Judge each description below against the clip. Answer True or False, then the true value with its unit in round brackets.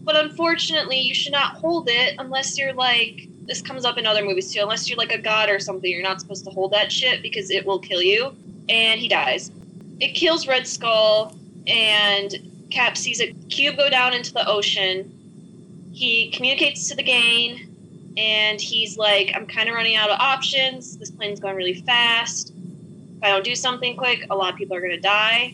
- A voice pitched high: True (210 Hz)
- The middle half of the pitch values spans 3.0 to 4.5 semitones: True (4.1 semitones)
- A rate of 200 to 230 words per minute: True (205 wpm)